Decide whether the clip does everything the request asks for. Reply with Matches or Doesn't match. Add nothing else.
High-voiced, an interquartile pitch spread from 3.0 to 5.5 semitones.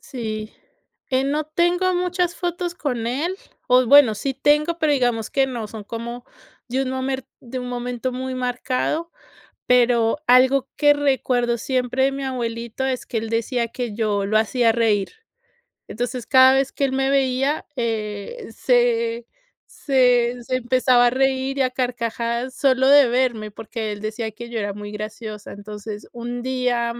Doesn't match